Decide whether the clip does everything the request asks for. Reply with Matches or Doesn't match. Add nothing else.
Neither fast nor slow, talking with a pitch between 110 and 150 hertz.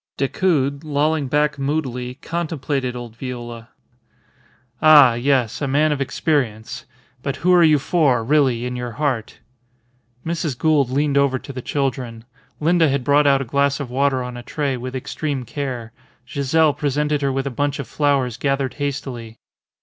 Matches